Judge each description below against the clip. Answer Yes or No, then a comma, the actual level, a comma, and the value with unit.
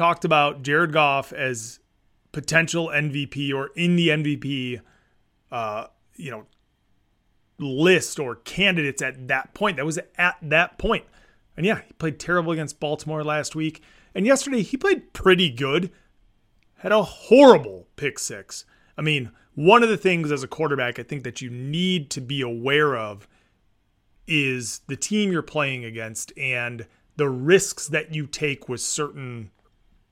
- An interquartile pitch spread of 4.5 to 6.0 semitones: Yes, average, 5.1 semitones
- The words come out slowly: No, average, 155 wpm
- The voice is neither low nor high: Yes, medium, 145 Hz